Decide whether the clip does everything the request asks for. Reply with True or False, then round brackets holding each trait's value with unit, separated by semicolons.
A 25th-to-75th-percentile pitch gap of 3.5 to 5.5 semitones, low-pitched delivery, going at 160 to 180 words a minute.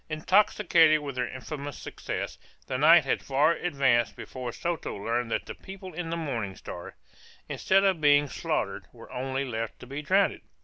False (4.8 semitones; 145 Hz; 170 wpm)